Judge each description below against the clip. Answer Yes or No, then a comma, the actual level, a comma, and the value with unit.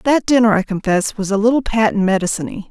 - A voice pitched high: Yes, high, 210 Hz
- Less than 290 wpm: Yes, average, 200 wpm